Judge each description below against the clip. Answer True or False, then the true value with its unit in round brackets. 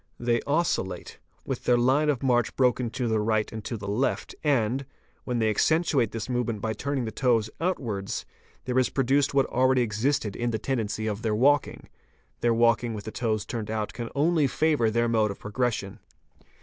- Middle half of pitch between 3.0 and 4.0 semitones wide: True (3.4 semitones)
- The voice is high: False (120 Hz)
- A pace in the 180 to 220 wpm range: True (190 wpm)